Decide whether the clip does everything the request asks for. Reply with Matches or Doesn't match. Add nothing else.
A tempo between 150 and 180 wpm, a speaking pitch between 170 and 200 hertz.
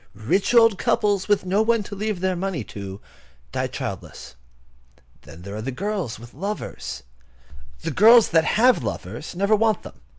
Matches